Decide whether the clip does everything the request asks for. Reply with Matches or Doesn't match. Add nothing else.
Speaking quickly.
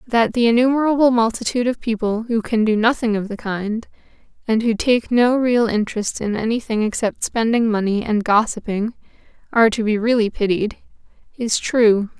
Doesn't match